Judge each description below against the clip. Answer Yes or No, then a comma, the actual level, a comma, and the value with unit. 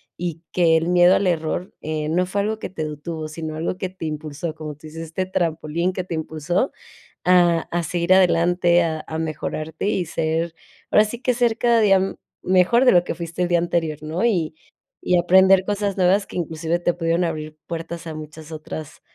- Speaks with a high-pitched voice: No, medium, 170 Hz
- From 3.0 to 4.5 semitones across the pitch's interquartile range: No, narrow, 2.6 semitones